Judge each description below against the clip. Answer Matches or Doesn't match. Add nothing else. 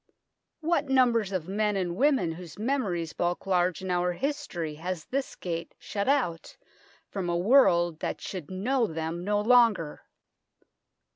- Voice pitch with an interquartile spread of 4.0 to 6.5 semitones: Matches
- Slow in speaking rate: Doesn't match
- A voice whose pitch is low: Doesn't match